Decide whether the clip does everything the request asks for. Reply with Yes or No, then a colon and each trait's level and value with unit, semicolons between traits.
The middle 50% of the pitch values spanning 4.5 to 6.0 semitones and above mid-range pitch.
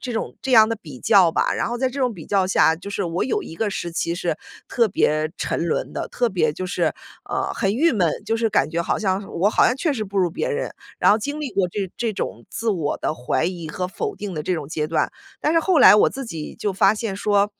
Yes: average, 5.2 semitones; high, 200 Hz